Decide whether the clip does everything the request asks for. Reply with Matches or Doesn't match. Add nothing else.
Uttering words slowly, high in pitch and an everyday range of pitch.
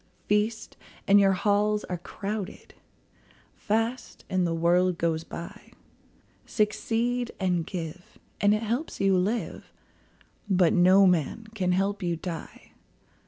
Matches